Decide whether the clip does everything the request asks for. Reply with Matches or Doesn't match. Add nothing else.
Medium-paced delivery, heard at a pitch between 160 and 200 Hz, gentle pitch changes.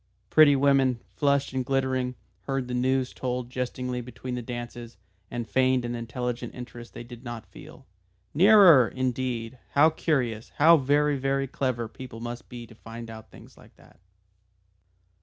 Doesn't match